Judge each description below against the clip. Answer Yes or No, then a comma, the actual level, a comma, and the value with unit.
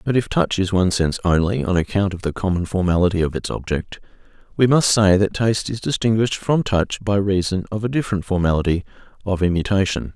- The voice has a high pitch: No, very low, 95 Hz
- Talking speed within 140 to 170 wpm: No, average, 195 wpm